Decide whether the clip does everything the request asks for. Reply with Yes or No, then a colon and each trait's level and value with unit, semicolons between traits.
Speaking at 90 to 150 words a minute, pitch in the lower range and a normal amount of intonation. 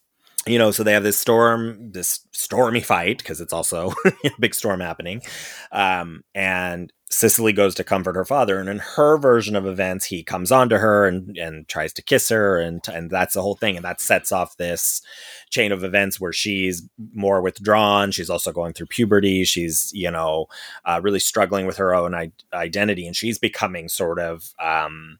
No: average, 195 wpm; very low, 95 Hz; average, 3.2 semitones